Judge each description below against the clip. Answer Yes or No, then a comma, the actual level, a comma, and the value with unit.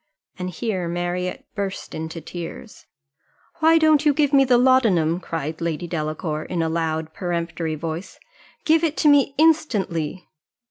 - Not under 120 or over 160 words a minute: Yes, average, 145 wpm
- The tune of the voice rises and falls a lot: Yes, wide, 8.2 semitones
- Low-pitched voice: No, medium, 180 Hz